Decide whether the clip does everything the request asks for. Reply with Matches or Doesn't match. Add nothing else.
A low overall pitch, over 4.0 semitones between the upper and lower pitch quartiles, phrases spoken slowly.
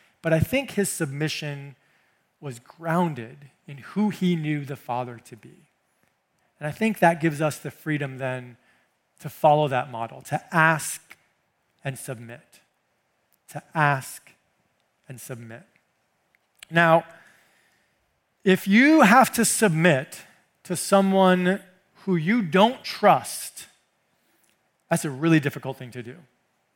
Doesn't match